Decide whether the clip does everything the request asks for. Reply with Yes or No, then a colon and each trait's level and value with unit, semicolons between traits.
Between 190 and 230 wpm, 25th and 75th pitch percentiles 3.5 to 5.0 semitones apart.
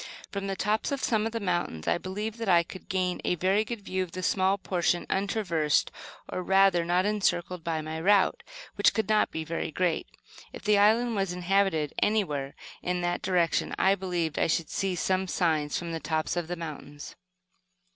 No: average, 195 wpm; average, 3.0 semitones